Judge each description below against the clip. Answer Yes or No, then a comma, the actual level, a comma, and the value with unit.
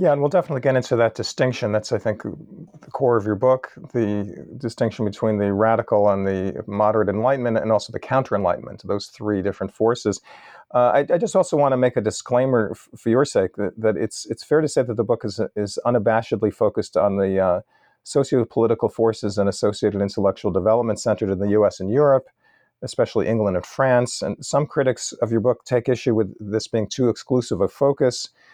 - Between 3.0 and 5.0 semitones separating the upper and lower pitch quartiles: Yes, average, 3.5 semitones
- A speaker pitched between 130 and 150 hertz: No, low, 115 Hz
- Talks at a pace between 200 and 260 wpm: Yes, fast, 205 wpm